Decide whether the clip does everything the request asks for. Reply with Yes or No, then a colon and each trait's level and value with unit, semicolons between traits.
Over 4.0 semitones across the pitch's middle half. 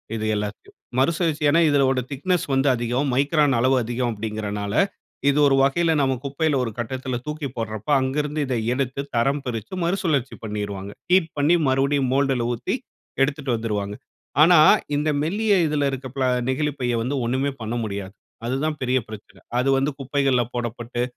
No: average, 3.6 semitones